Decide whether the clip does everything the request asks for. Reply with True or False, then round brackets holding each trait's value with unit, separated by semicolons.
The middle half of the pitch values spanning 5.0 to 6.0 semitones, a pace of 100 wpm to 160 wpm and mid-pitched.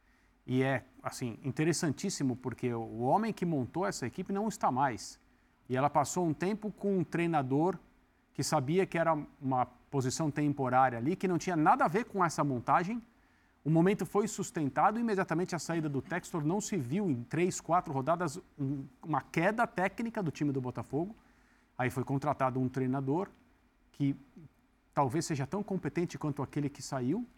False (5.5 semitones; 170 wpm; 155 Hz)